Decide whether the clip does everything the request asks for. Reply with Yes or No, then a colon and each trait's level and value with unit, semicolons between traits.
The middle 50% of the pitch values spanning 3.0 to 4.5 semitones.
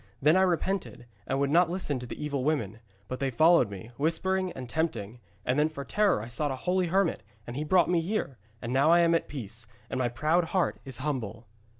No: wide, 5.4 semitones